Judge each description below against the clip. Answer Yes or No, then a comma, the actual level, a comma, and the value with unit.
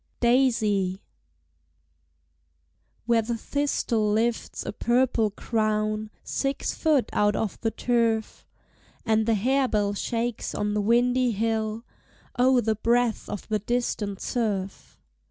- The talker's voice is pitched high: Yes, high, 225 Hz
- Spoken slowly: Yes, slow, 115 wpm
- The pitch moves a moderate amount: No, narrow, 2.3 semitones